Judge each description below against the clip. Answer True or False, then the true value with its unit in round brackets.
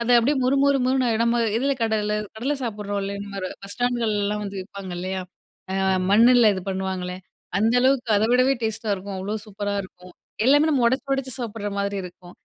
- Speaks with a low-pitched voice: False (215 Hz)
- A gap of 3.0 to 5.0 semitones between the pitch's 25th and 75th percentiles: True (3.7 semitones)